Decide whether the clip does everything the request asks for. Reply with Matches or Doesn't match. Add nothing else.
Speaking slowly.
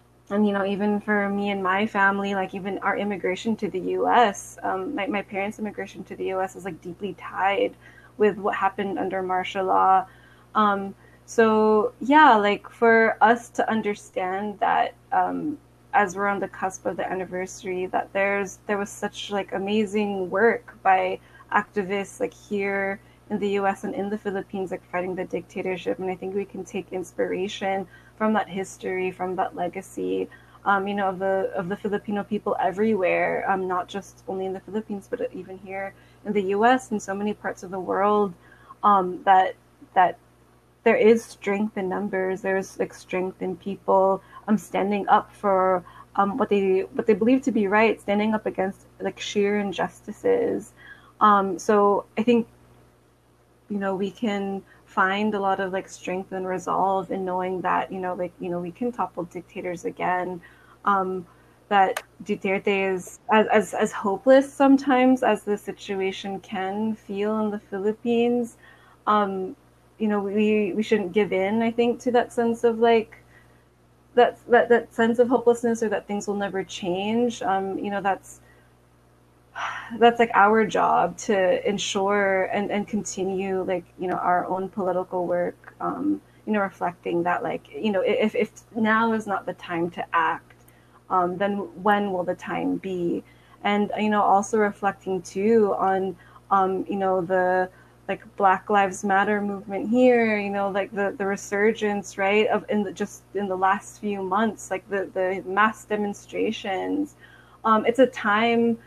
Doesn't match